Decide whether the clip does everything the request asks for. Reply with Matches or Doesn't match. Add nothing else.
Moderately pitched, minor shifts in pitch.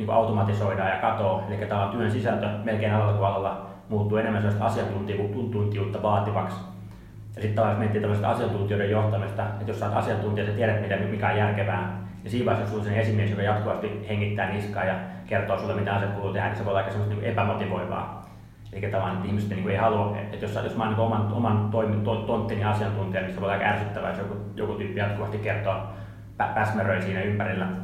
Doesn't match